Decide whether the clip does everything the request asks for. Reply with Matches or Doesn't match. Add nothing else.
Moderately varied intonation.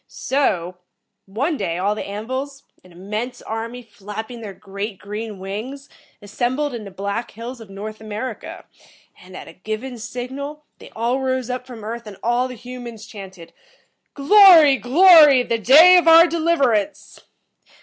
Matches